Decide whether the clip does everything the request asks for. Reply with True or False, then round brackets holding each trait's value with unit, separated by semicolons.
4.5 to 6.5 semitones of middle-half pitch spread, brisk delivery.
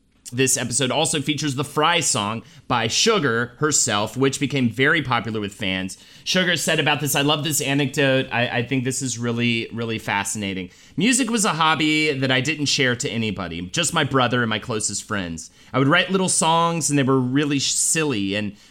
False (5.0 semitones; 195 wpm)